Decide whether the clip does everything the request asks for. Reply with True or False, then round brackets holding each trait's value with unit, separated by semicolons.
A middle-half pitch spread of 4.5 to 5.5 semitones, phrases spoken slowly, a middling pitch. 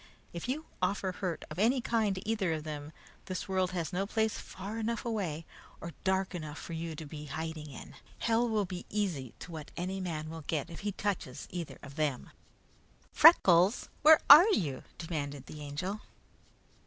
False (4.9 semitones; 180 wpm; 180 Hz)